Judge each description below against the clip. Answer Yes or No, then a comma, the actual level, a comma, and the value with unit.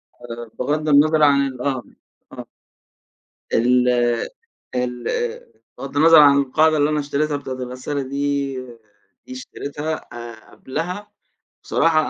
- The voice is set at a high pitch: No, medium, 140 Hz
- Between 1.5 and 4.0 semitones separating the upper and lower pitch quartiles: Yes, average, 3.1 semitones